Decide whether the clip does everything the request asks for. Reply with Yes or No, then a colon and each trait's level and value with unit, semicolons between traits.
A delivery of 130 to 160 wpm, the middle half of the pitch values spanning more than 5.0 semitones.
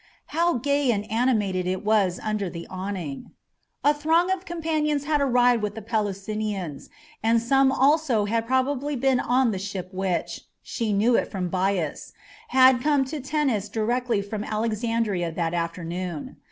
Yes: average, 155 wpm; wide, 5.5 semitones